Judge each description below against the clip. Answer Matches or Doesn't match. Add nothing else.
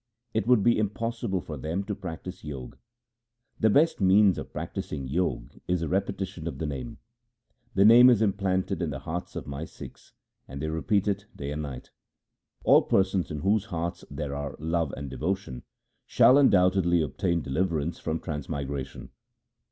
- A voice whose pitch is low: Matches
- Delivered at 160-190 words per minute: Matches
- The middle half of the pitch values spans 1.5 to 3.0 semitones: Doesn't match